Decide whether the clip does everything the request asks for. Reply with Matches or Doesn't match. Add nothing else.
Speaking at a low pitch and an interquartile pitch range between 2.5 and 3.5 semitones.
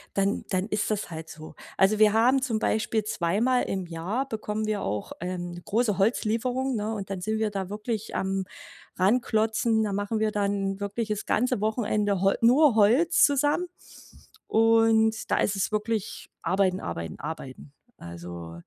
Doesn't match